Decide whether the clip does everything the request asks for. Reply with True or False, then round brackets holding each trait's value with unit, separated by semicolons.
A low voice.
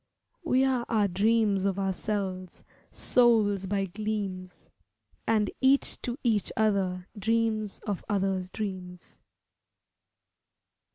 False (205 Hz)